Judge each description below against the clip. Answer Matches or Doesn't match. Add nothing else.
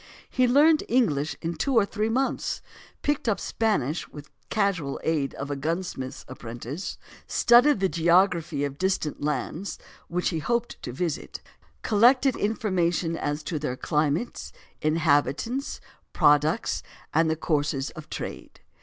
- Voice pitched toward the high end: Doesn't match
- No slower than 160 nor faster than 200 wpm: Doesn't match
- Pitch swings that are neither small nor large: Doesn't match